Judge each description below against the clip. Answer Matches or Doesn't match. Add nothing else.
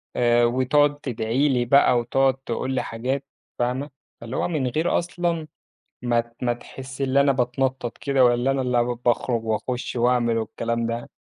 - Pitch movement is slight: Matches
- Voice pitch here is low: Matches